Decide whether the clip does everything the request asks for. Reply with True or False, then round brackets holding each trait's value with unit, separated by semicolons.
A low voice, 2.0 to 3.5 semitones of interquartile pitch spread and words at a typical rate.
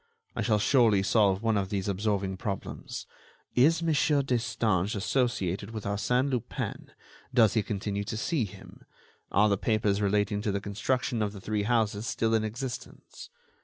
True (105 Hz; 3.0 semitones; 160 wpm)